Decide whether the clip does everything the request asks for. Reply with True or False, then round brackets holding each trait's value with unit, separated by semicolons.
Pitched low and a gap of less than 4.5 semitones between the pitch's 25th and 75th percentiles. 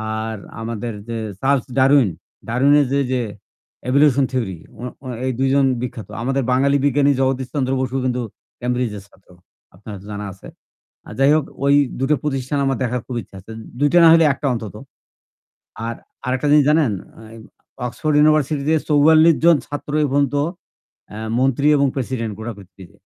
True (130 Hz; 3.6 semitones)